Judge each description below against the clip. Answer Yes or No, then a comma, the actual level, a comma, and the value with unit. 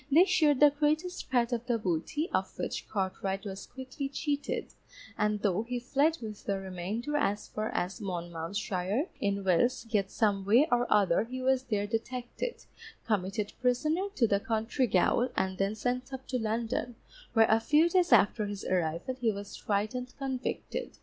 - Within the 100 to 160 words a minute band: No, average, 170 wpm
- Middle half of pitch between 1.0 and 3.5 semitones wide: No, average, 4.6 semitones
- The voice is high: Yes, high, 225 Hz